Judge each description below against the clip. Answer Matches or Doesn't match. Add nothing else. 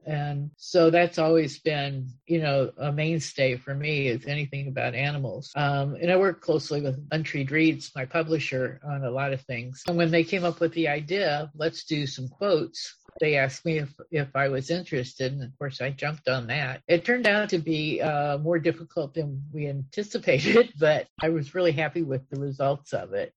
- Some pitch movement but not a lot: Matches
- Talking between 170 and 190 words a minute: Doesn't match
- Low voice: Doesn't match